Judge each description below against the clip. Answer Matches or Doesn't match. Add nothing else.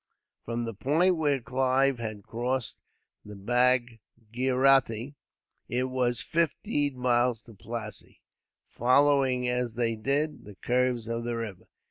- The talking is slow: Matches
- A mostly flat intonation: Matches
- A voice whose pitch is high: Doesn't match